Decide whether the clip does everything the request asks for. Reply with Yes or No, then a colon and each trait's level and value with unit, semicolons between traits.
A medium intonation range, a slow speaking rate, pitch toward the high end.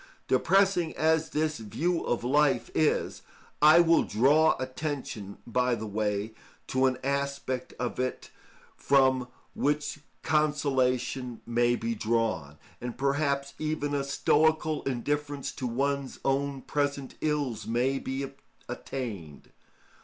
No: average, 3.4 semitones; slow, 115 wpm; low, 135 Hz